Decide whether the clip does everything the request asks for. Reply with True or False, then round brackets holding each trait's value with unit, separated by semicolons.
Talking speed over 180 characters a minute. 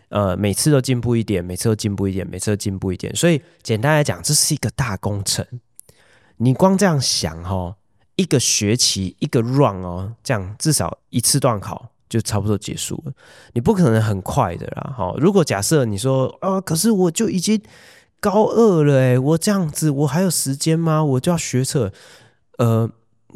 True (285 characters per minute)